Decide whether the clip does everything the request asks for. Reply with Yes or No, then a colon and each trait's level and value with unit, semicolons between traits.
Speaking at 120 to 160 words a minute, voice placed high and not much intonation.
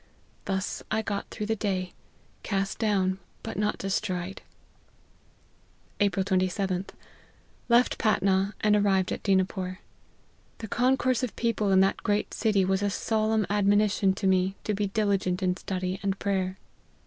Yes: average, 150 wpm; high, 195 Hz; narrow, 1.8 semitones